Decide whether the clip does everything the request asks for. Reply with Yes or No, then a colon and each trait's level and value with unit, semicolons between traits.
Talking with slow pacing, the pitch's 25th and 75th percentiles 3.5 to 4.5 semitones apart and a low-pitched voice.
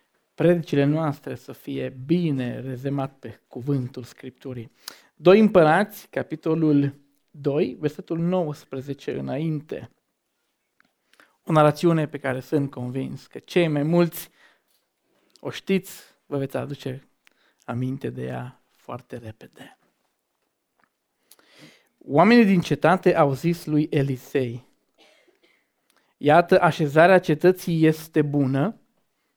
No: slow, 100 wpm; average, 4.0 semitones; medium, 150 Hz